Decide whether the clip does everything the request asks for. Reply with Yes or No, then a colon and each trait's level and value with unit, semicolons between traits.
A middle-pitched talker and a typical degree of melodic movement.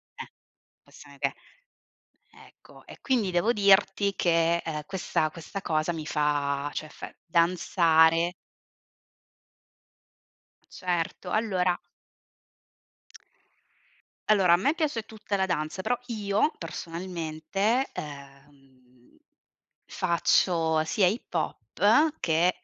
Yes: medium, 175 Hz; average, 4.2 semitones